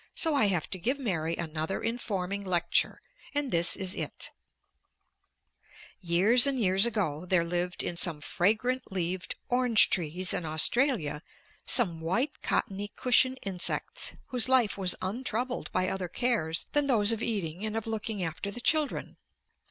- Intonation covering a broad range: Yes, wide, 5.7 semitones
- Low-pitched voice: No, high, 195 Hz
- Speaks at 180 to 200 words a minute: No, average, 150 wpm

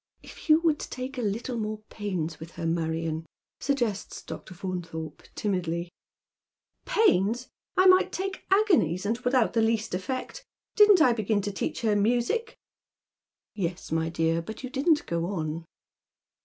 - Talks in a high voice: Yes, high, 210 Hz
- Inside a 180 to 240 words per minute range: No, average, 155 wpm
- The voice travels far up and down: Yes, wide, 7.2 semitones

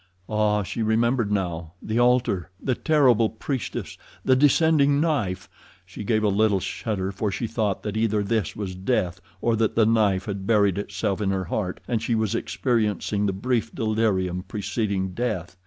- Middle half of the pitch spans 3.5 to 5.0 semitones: No, average, 3.1 semitones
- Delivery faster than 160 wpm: Yes, average, 170 wpm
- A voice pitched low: Yes, low, 105 Hz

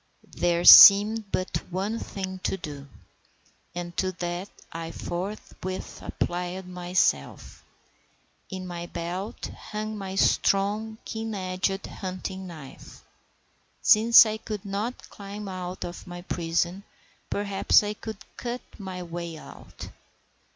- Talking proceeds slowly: Yes, slow, 115 wpm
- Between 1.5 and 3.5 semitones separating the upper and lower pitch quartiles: Yes, average, 2.7 semitones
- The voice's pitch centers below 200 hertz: Yes, medium, 185 Hz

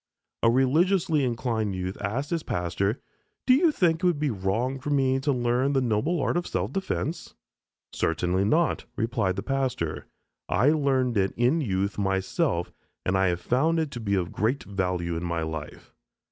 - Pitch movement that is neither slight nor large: No, wide, 7.1 semitones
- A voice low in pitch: Yes, low, 120 Hz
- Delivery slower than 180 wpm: Yes, average, 170 wpm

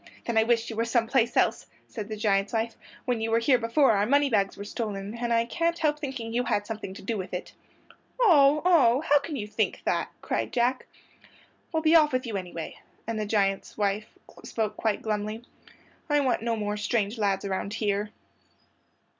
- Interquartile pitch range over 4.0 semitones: No, average, 3.6 semitones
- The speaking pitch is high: Yes, high, 225 Hz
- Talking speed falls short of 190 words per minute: No, average, 195 wpm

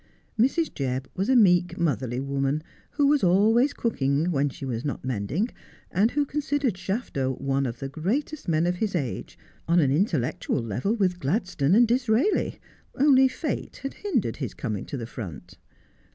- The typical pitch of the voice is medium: Yes, medium, 175 Hz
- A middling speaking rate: Yes, average, 165 wpm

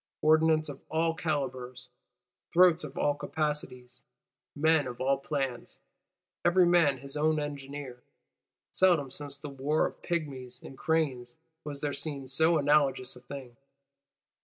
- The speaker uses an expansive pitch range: No, average, 3.0 semitones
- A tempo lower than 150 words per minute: Yes, slow, 135 wpm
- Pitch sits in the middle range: Yes, medium, 145 Hz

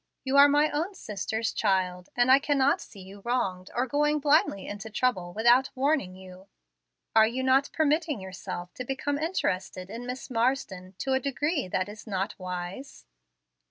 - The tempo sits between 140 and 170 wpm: Yes, average, 165 wpm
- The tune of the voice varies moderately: No, wide, 6.7 semitones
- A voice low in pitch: No, high, 240 Hz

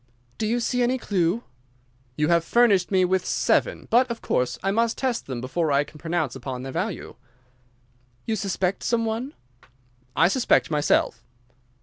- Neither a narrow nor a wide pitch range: No, wide, 7.4 semitones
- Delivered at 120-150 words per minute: No, average, 160 wpm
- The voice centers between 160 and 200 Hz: Yes, high, 190 Hz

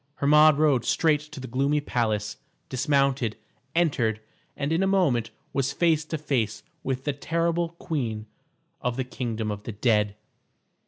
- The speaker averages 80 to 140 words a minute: No, average, 150 wpm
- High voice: No, low, 135 Hz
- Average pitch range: Yes, average, 4.9 semitones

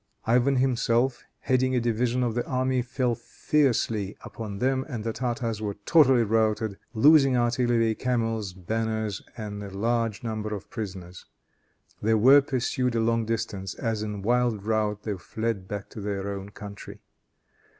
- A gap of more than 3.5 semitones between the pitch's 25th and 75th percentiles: No, average, 2.9 semitones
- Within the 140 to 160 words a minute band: Yes, average, 150 wpm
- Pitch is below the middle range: Yes, low, 115 Hz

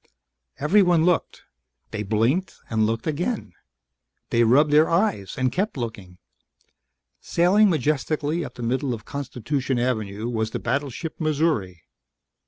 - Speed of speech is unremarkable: No, slow, 125 wpm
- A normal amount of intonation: No, wide, 6.1 semitones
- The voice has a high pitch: No, low, 135 Hz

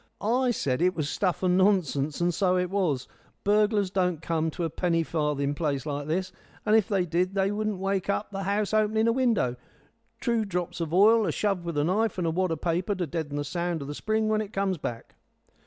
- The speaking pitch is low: No, medium, 180 Hz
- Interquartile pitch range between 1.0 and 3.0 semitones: No, average, 4.0 semitones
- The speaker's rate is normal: No, fast, 225 wpm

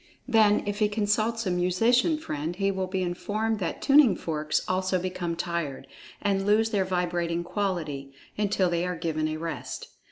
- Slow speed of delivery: No, average, 165 wpm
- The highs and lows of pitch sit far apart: No, average, 3.5 semitones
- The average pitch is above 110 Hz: Yes, medium, 185 Hz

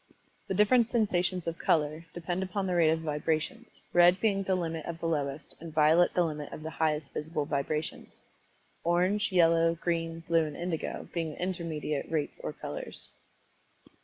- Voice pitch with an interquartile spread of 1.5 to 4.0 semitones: Yes, narrow, 2.4 semitones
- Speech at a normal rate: Yes, average, 170 wpm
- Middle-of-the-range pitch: Yes, medium, 165 Hz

